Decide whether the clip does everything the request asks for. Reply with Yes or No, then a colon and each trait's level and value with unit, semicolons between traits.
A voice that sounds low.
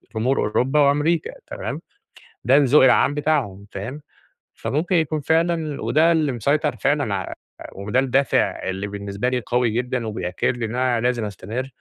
Yes: low, 130 Hz